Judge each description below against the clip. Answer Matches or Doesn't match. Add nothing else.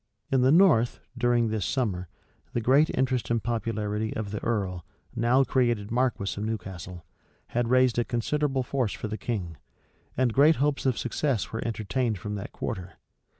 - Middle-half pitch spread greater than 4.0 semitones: Doesn't match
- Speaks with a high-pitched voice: Doesn't match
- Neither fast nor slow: Matches